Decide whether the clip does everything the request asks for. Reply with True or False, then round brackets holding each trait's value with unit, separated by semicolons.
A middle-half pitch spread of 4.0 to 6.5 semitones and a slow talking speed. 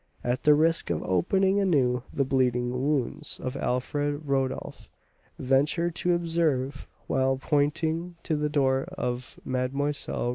False (3.6 semitones; 130 wpm)